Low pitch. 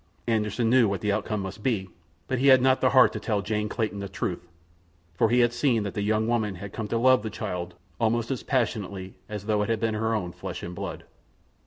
Yes: low, 110 Hz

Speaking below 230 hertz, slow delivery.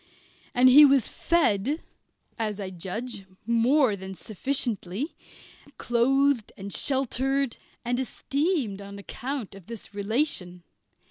No: high, 235 Hz; slow, 105 wpm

